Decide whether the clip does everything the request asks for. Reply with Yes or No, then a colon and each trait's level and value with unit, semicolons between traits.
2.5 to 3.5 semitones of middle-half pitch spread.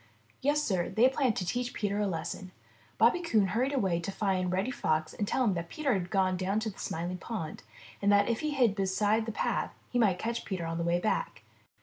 No: average, 4.3 semitones